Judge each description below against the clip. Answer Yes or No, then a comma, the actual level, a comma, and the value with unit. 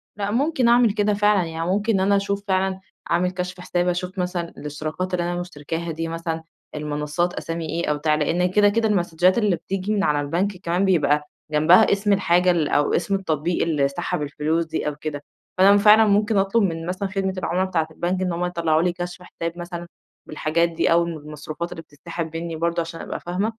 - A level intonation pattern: No, average, 3.0 semitones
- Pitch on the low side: No, medium, 175 Hz